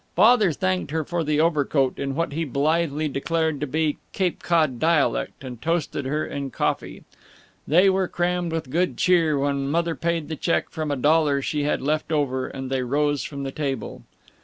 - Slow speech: No, average, 185 wpm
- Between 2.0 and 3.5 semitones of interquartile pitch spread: Yes, average, 3.1 semitones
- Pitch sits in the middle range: Yes, medium, 150 Hz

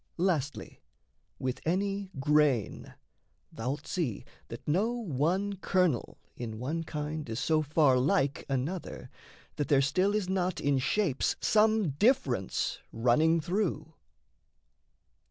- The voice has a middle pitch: Yes, medium, 155 Hz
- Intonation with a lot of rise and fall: Yes, wide, 5.7 semitones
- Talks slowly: Yes, slow, 115 wpm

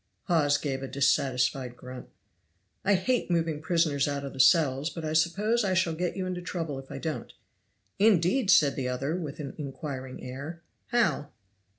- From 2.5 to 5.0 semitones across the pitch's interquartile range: Yes, average, 4.5 semitones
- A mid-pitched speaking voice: Yes, medium, 155 Hz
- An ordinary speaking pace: Yes, average, 175 wpm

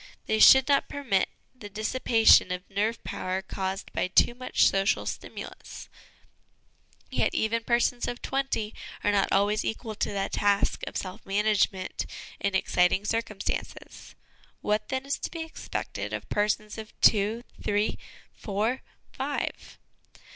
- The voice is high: Yes, high, 210 Hz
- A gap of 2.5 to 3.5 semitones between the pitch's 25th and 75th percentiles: Yes, average, 3.0 semitones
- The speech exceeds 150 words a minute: No, average, 140 wpm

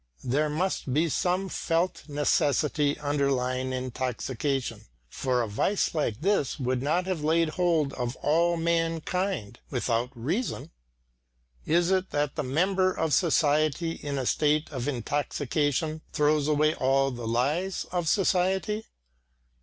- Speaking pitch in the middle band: Yes, medium, 150 Hz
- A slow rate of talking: Yes, slow, 130 wpm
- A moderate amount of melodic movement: Yes, average, 4.4 semitones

